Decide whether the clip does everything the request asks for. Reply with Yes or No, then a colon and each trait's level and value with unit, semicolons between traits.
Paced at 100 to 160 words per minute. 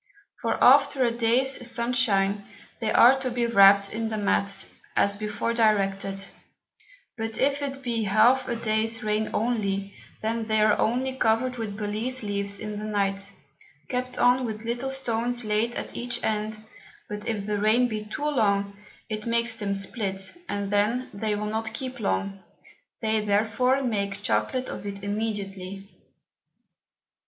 Yes: average, 155 wpm